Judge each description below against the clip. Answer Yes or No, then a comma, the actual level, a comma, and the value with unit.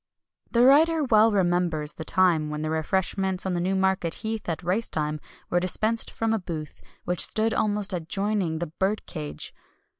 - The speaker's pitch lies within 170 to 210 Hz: Yes, medium, 185 Hz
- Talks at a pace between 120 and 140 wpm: No, average, 155 wpm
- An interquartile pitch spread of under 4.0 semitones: No, average, 4.7 semitones